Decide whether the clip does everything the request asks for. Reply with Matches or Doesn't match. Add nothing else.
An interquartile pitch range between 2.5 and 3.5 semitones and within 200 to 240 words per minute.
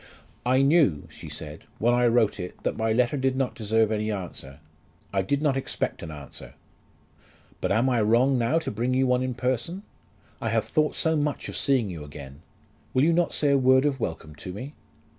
Doesn't match